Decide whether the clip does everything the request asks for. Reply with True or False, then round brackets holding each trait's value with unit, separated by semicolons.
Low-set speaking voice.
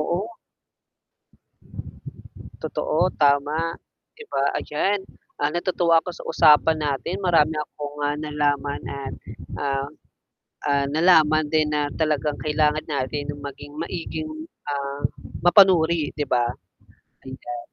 False (150 Hz)